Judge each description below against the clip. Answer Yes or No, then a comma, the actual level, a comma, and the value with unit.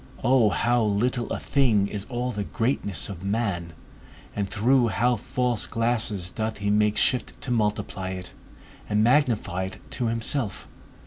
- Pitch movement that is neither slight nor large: Yes, average, 3.3 semitones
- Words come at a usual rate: Yes, average, 150 wpm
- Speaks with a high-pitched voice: No, low, 110 Hz